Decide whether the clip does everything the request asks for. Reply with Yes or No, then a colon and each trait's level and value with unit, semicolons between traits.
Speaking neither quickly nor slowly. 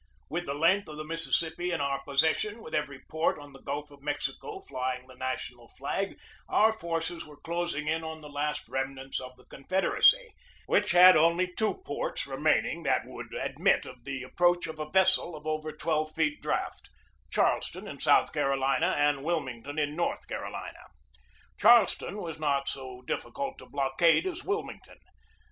Yes: average, 170 wpm